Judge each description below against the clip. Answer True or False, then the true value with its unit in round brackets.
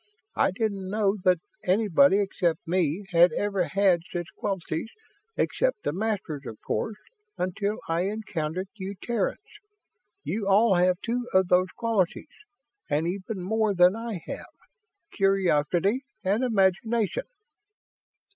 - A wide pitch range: False (3.3 semitones)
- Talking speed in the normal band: False (125 wpm)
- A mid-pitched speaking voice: False (195 Hz)